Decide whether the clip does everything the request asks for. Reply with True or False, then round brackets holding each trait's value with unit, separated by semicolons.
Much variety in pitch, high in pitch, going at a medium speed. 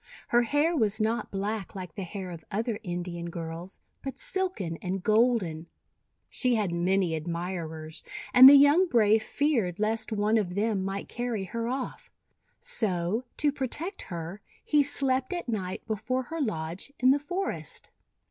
True (6.3 semitones; 215 Hz; 155 wpm)